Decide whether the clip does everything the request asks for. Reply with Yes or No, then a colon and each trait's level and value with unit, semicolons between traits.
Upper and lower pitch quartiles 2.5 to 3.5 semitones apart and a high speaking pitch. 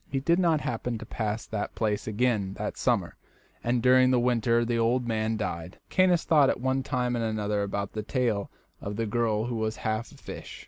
No: average, 2.8 semitones; low, 115 Hz